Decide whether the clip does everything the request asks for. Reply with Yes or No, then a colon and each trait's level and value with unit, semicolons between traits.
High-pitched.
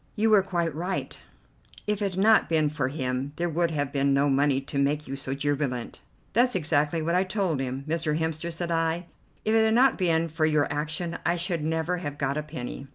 No: medium, 160 Hz